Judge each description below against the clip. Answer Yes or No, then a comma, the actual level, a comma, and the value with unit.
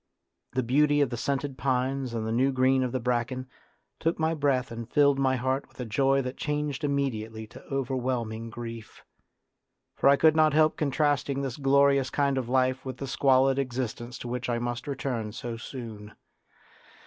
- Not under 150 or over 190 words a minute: Yes, average, 180 wpm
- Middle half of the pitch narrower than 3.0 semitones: Yes, narrow, 2.6 semitones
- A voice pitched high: No, low, 130 Hz